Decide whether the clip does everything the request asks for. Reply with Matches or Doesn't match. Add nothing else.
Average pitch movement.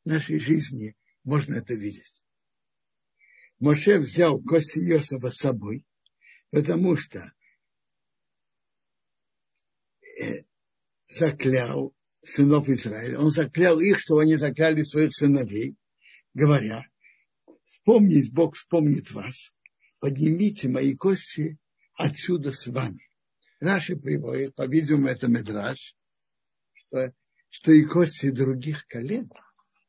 Matches